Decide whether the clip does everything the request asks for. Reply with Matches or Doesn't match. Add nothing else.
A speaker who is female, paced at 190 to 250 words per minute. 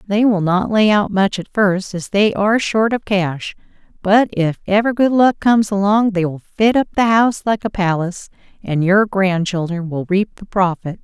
Matches